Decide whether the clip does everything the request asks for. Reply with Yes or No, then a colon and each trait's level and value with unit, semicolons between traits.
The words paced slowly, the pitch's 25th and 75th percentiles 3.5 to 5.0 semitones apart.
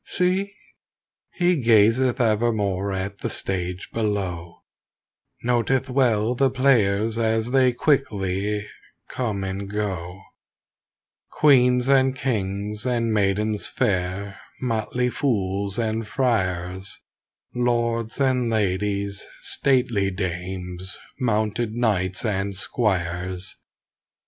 Yes: slow, 90 wpm; average, 4.1 semitones